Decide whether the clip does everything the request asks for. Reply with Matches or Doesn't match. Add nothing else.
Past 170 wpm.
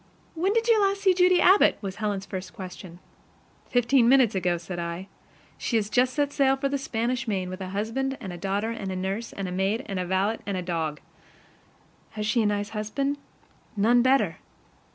Matches